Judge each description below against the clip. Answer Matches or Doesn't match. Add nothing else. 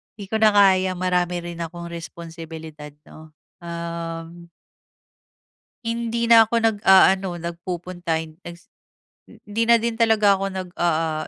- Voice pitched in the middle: Matches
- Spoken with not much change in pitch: Doesn't match